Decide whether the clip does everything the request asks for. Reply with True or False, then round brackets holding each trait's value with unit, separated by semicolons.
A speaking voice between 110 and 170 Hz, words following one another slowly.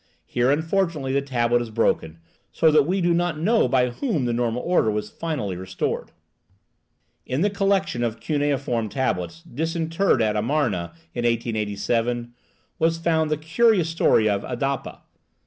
False (135 Hz; 145 wpm)